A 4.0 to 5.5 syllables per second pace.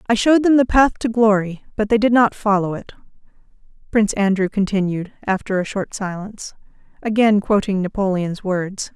Yes: 5.4 syllables/s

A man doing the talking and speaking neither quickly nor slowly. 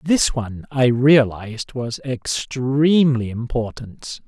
No: male; slow, 100 wpm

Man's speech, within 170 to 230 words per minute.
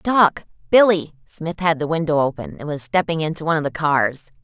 No: female; fast, 205 wpm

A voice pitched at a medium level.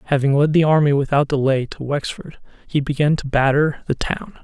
Yes: medium, 145 Hz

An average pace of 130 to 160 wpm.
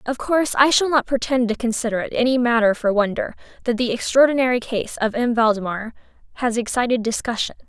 No: average, 180 wpm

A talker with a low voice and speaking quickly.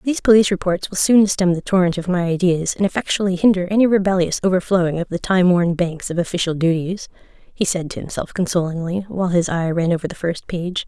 No: medium, 180 Hz; fast, 210 wpm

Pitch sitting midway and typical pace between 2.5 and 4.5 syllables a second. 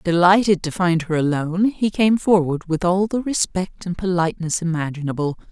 No: medium, 180 Hz; 5.3 syllables/s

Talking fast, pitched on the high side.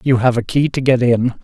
No: fast, 295 wpm; low, 125 Hz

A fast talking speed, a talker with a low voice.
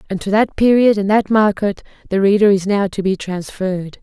No: fast, 210 wpm; high, 200 Hz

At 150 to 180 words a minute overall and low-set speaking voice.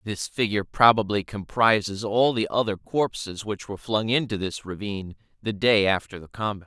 Yes: average, 170 wpm; low, 105 Hz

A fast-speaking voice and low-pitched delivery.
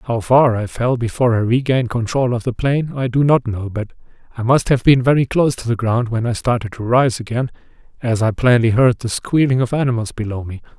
Yes: fast, 230 wpm; low, 120 Hz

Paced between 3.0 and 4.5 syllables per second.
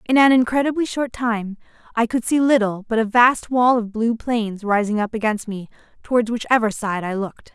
No: 5.2 syllables/s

